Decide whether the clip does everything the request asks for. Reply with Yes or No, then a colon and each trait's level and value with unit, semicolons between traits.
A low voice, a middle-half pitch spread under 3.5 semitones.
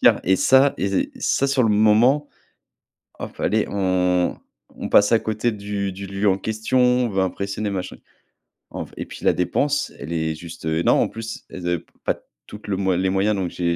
Yes: low, 100 Hz; average, 3.1 semitones